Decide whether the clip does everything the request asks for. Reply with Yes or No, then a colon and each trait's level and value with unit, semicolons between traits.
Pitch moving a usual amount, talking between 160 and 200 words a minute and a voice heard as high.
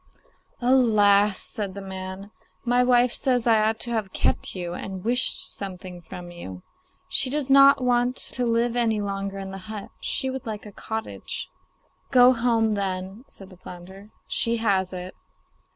Yes: average, 4.2 semitones; average, 165 wpm; high, 210 Hz